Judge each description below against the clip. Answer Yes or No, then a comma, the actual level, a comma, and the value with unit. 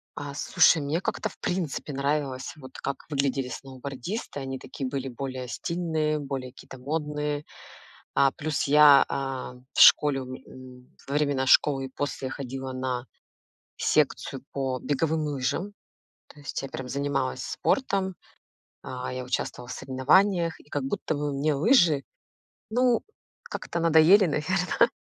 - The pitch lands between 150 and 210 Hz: No, medium, 140 Hz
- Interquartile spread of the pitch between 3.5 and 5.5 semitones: No, average, 2.8 semitones